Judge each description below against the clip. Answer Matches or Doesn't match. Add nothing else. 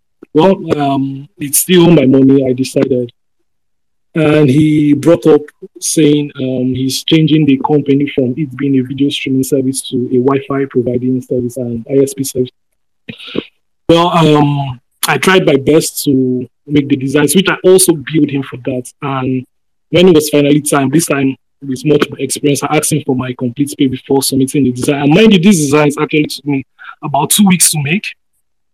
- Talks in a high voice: Doesn't match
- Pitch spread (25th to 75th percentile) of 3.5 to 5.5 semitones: Doesn't match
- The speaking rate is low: Doesn't match